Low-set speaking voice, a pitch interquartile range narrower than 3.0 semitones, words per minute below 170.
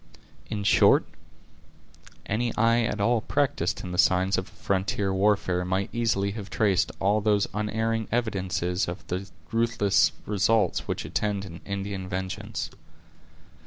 Yes: low, 100 Hz; narrow, 2.6 semitones; slow, 135 wpm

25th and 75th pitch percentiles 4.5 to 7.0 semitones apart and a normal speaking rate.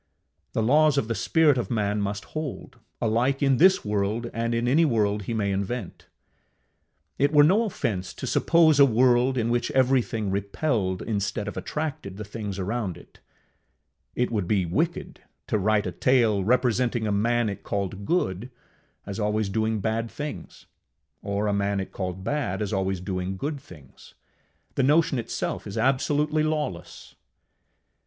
Yes: average, 5.0 semitones; average, 160 wpm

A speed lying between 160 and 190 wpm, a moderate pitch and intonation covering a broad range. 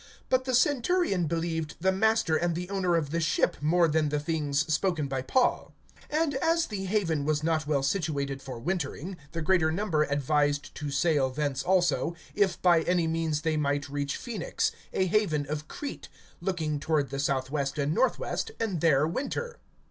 No: average, 175 wpm; medium, 160 Hz; average, 4.4 semitones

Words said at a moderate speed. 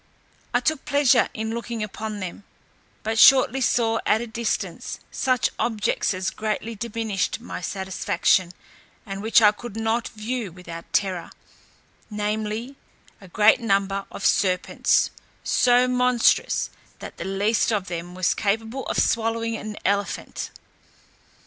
No: slow, 130 wpm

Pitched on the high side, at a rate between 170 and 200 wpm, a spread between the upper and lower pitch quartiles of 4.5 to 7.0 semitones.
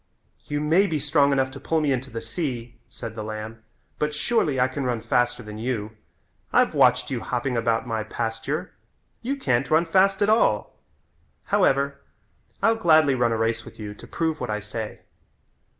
No: low, 130 Hz; average, 180 wpm; average, 5.1 semitones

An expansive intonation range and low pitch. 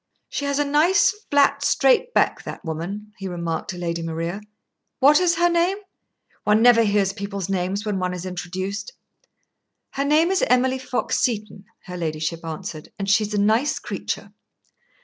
No: wide, 7.4 semitones; high, 205 Hz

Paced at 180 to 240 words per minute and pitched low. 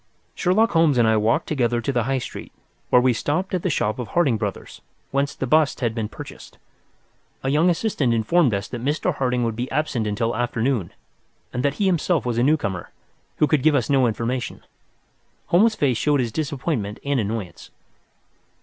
Yes: average, 185 wpm; low, 130 Hz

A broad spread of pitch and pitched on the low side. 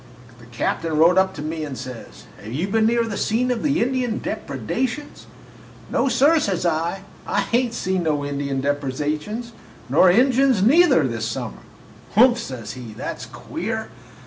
No: wide, 8.7 semitones; medium, 185 Hz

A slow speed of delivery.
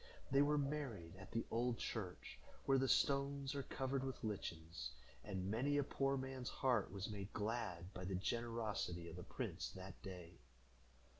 No: average, 165 wpm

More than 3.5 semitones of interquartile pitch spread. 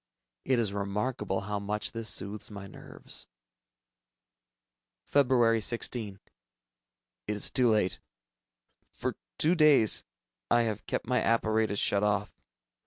No: average, 2.7 semitones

